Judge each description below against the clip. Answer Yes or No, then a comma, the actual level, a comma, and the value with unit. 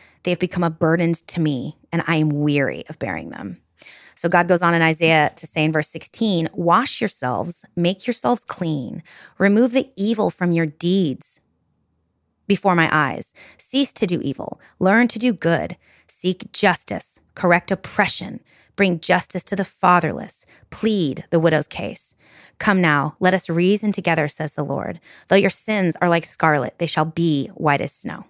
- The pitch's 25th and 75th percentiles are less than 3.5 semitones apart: No, average, 3.8 semitones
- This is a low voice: No, medium, 170 Hz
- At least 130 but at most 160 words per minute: No, average, 170 wpm